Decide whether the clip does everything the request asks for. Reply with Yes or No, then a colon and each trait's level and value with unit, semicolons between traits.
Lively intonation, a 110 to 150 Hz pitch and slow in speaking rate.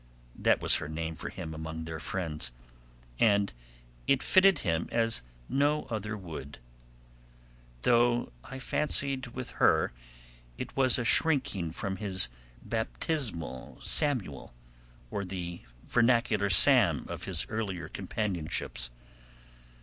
No: wide, 6.8 semitones; low, 100 Hz; slow, 115 wpm